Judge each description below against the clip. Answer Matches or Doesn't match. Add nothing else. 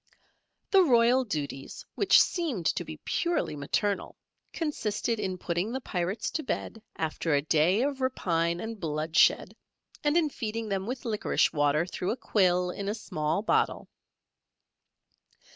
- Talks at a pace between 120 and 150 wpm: Matches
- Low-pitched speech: Doesn't match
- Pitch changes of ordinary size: Doesn't match